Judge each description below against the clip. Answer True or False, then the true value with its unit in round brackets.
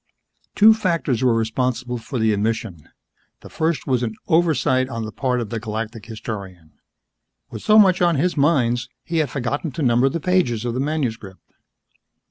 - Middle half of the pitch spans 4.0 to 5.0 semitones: False (5.6 semitones)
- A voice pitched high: False (125 Hz)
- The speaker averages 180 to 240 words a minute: False (170 wpm)